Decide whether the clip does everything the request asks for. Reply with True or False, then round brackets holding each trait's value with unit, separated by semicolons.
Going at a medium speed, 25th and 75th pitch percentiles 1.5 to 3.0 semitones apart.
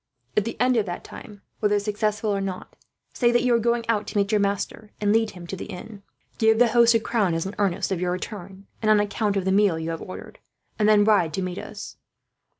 False (250 wpm; 2.6 semitones)